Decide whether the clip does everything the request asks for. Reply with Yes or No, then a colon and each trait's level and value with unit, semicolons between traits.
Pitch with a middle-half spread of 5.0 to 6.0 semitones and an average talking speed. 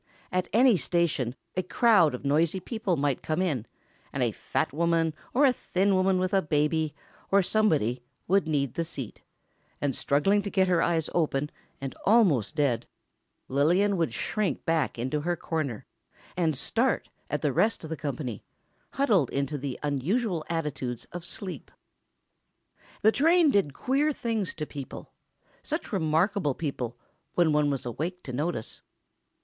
Yes: average, 5.3 semitones; average, 155 wpm